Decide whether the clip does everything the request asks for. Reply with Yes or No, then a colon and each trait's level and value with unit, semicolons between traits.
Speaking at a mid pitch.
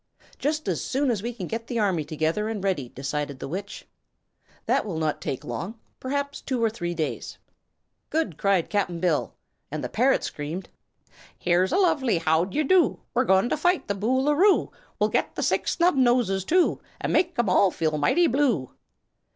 No: high, 205 Hz